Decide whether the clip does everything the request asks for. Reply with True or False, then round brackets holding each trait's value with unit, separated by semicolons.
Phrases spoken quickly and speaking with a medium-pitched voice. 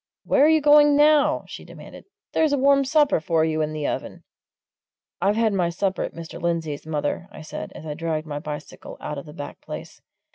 True (210 wpm; 170 Hz)